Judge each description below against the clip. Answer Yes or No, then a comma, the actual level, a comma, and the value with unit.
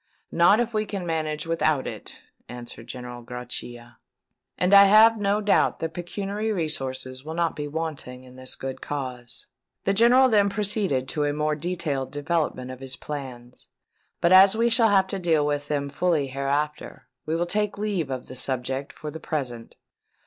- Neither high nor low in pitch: Yes, medium, 155 Hz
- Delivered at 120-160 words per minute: No, average, 175 wpm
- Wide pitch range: Yes, wide, 6.7 semitones